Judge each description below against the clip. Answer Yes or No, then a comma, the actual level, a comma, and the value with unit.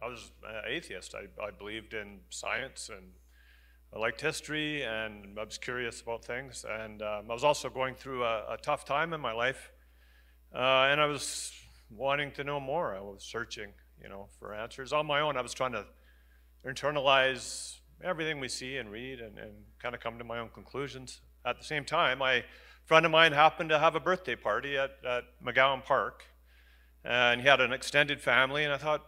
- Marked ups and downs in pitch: Yes, wide, 5.9 semitones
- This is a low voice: Yes, low, 120 Hz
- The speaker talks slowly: No, average, 200 wpm